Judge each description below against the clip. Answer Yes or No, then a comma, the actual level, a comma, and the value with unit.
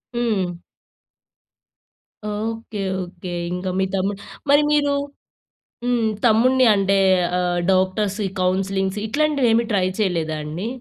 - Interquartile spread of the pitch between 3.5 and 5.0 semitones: Yes, average, 3.8 semitones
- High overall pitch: Yes, high, 200 Hz